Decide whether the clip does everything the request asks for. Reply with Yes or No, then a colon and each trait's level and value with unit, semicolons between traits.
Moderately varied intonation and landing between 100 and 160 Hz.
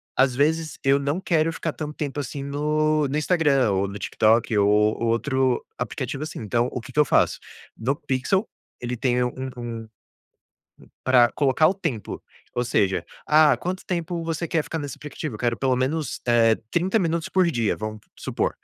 Yes: average, 4.6 semitones; medium, 140 Hz